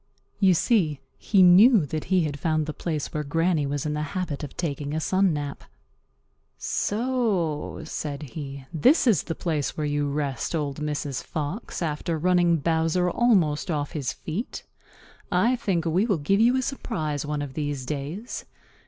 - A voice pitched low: No, medium, 155 Hz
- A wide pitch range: No, average, 4.0 semitones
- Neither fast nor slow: Yes, average, 170 wpm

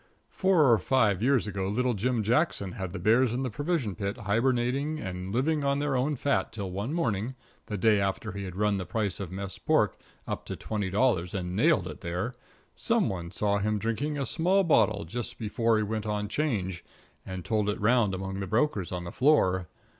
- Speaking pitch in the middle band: No, low, 105 Hz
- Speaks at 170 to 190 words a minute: No, fast, 205 wpm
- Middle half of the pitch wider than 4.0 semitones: Yes, average, 4.9 semitones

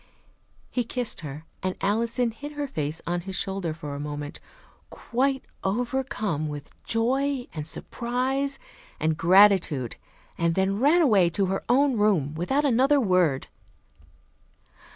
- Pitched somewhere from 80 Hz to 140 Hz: No, high, 200 Hz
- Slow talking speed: Yes, slow, 130 wpm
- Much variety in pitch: Yes, wide, 7.6 semitones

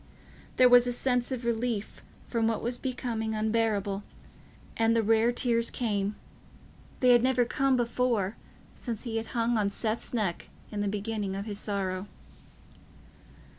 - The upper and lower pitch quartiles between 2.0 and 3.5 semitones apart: Yes, average, 2.7 semitones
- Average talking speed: Yes, average, 145 wpm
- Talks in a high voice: Yes, high, 225 Hz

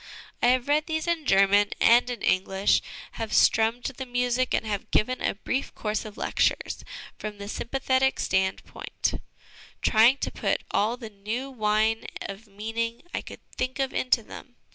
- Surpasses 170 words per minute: No, average, 165 wpm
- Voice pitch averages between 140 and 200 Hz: No, high, 230 Hz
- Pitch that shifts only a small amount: No, average, 3.4 semitones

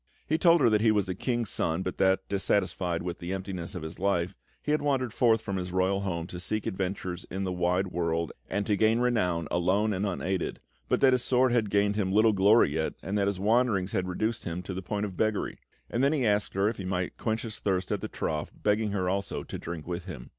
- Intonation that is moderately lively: Yes, average, 3.2 semitones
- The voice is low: Yes, very low, 95 Hz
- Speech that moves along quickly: Yes, fast, 245 wpm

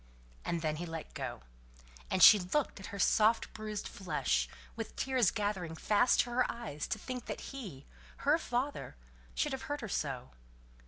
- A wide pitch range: Yes, wide, 6.9 semitones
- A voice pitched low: No, high, 210 Hz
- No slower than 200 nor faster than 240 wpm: No, average, 170 wpm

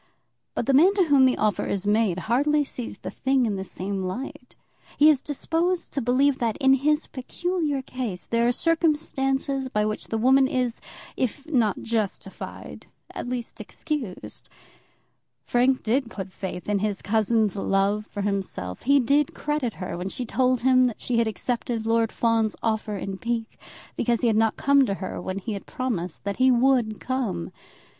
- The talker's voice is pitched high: Yes, high, 240 Hz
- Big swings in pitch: No, average, 4.2 semitones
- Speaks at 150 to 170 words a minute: No, average, 180 wpm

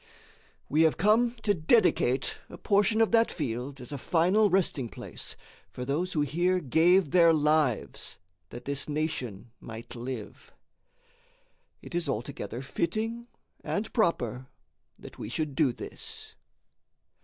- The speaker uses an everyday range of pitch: No, wide, 6.4 semitones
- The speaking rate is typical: No, slow, 130 wpm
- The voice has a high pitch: No, medium, 155 Hz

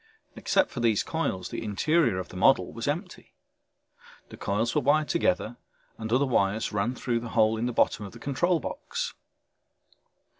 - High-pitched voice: No, low, 120 Hz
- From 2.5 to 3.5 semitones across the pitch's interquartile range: No, wide, 5.6 semitones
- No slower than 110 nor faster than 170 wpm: No, average, 180 wpm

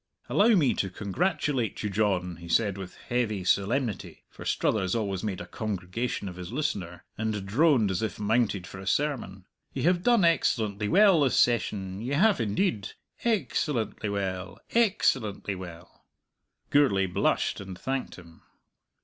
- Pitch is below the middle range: Yes, low, 105 Hz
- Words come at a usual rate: Yes, average, 155 wpm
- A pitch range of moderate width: No, wide, 6.2 semitones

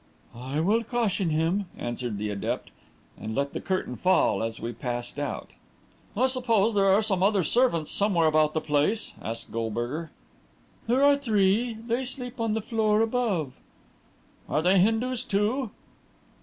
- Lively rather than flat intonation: Yes, wide, 7.7 semitones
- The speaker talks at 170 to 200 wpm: No, average, 155 wpm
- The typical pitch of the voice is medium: No, high, 195 Hz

